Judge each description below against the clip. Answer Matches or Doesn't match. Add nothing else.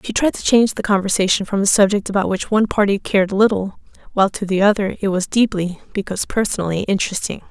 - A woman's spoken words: Matches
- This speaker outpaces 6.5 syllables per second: Matches